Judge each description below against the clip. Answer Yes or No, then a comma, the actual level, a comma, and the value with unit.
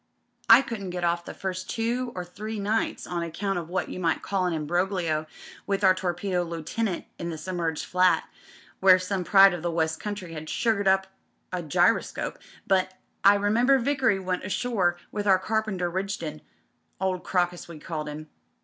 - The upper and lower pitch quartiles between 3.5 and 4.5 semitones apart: No, average, 2.8 semitones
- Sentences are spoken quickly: No, average, 175 wpm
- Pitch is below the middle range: No, medium, 185 Hz